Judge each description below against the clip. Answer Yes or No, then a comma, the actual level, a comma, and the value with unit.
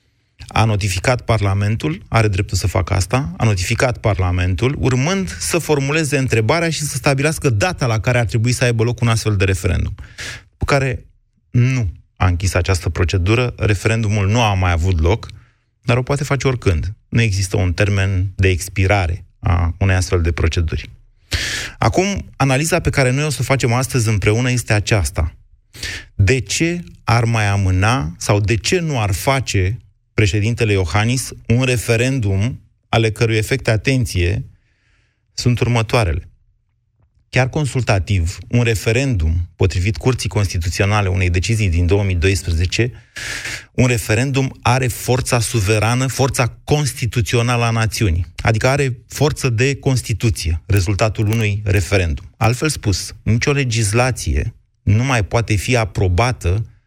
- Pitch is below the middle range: Yes, low, 110 Hz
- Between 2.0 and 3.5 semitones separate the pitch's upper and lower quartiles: No, average, 4.1 semitones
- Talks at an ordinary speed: Yes, average, 135 wpm